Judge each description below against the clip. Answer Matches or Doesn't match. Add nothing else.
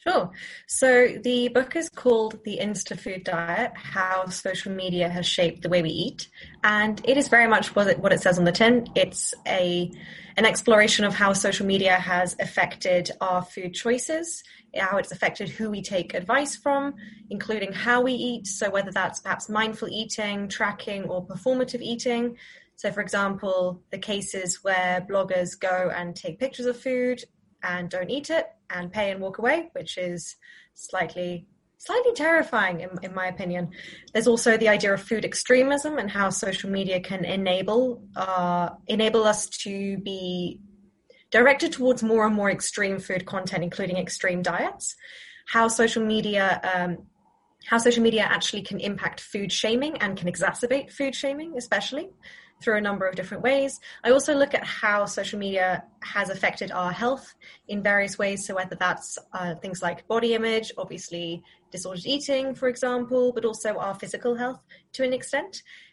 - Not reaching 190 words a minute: Matches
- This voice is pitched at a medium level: Doesn't match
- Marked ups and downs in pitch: Doesn't match